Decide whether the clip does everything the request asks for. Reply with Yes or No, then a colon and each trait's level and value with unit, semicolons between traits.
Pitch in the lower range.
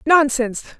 No: very high, 275 Hz